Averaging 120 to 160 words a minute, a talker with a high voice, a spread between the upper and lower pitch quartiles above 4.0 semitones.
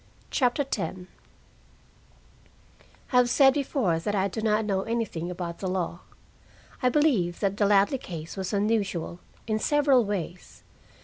Yes: average, 140 wpm; high, 205 Hz; average, 5.1 semitones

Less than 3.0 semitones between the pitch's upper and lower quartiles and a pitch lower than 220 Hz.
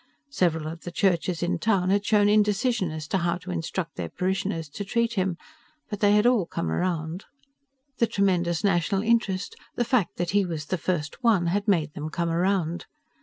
No: average, 3.4 semitones; medium, 185 Hz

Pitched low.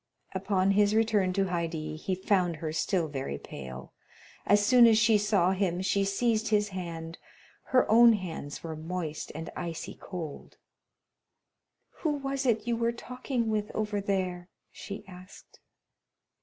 No: high, 195 Hz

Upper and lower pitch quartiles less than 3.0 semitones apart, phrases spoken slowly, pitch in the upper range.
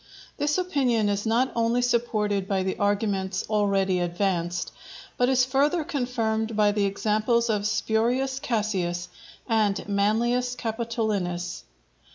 No: average, 3.4 semitones; slow, 120 wpm; high, 220 Hz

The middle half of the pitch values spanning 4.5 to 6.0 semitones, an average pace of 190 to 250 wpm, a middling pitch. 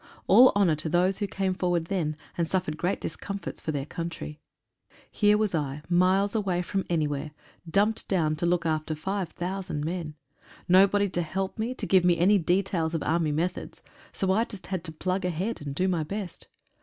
No: average, 3.3 semitones; average, 195 wpm; medium, 180 Hz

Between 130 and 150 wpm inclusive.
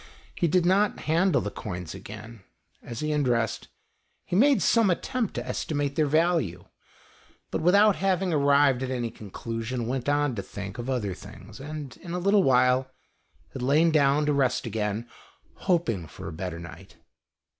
No: average, 165 wpm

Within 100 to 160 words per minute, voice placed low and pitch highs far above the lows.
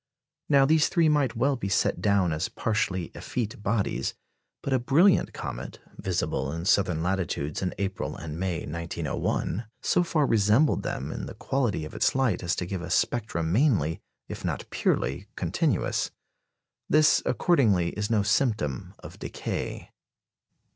Yes: average, 150 wpm; low, 105 Hz; wide, 7.5 semitones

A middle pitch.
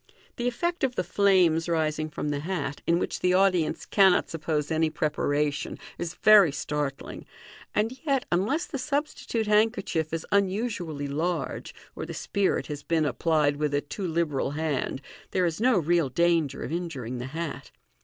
Yes: medium, 165 Hz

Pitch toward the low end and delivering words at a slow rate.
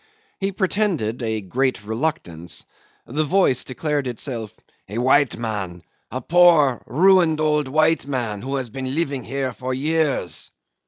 Yes: low, 130 Hz; slow, 130 wpm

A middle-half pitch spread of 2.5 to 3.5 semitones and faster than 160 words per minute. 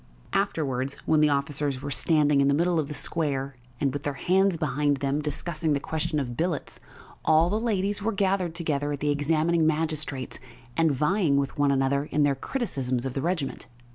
Yes: average, 3.1 semitones; average, 190 wpm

